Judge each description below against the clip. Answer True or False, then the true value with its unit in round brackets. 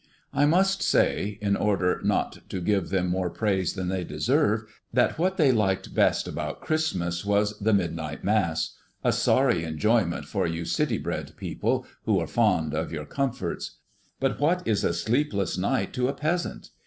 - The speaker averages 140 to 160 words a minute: False (170 wpm)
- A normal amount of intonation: False (6.2 semitones)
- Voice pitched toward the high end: False (100 Hz)